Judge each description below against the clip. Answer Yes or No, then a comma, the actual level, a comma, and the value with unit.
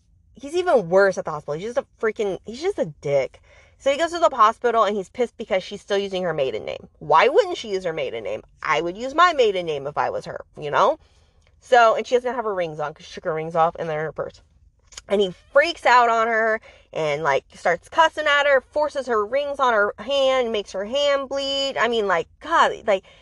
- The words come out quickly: Yes, fast, 245 wpm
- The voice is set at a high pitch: Yes, high, 240 Hz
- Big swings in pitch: Yes, wide, 6.8 semitones